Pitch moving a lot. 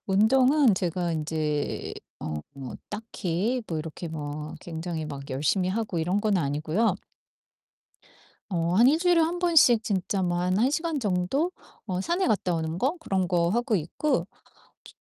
Yes: wide, 6.5 semitones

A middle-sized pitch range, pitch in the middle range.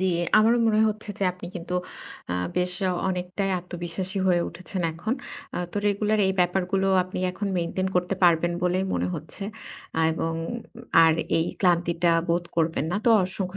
No: narrow, 2.1 semitones; medium, 180 Hz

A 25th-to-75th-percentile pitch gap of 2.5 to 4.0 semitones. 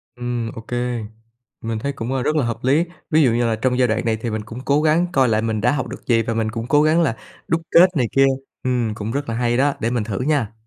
Yes: average, 3.5 semitones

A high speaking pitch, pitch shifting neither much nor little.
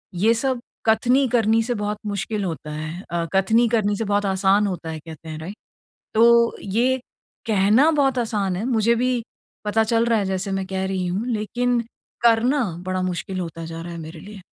Yes: high, 205 Hz; average, 4.0 semitones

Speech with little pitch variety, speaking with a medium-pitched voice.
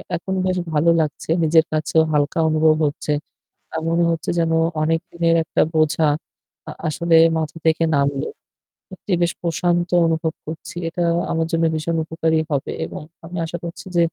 Yes: narrow, 1.5 semitones; medium, 160 Hz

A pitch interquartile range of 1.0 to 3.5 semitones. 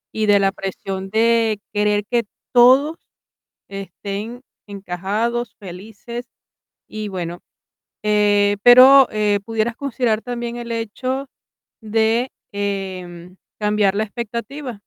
Yes: average, 2.9 semitones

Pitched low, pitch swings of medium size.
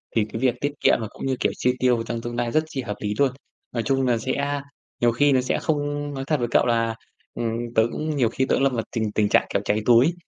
Yes: low, 125 Hz; average, 3.4 semitones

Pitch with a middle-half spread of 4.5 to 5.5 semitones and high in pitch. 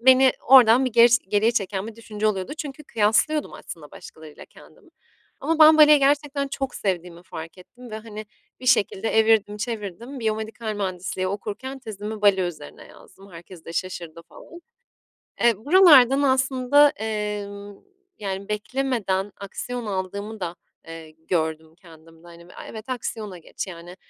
Yes: average, 5.1 semitones; high, 210 Hz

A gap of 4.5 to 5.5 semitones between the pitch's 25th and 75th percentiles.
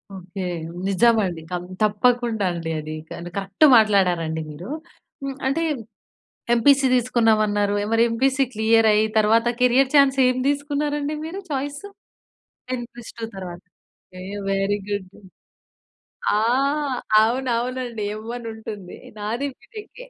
Yes: average, 4.8 semitones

